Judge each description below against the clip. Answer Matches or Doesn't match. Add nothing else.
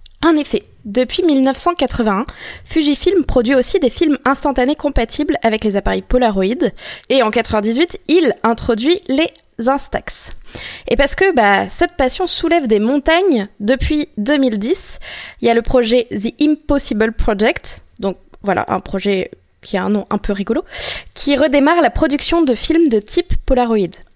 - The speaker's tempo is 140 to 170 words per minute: Matches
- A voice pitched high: Matches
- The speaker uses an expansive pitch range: Matches